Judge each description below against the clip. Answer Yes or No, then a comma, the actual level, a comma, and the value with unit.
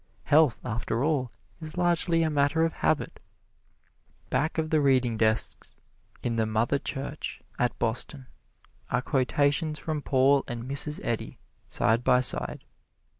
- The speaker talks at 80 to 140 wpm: Yes, slow, 135 wpm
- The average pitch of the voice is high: No, low, 135 Hz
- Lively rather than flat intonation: No, average, 4.4 semitones